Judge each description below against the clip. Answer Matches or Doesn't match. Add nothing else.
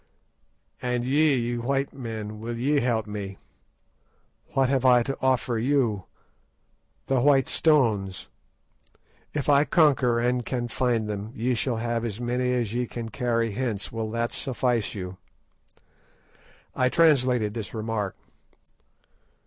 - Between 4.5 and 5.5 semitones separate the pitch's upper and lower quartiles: Doesn't match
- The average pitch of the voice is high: Doesn't match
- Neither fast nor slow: Doesn't match